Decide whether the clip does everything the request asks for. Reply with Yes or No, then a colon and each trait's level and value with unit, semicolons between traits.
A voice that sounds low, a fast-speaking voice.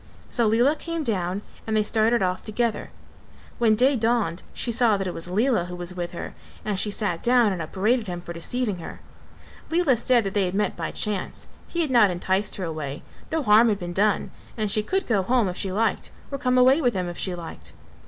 No: high, 210 Hz; fast, 220 wpm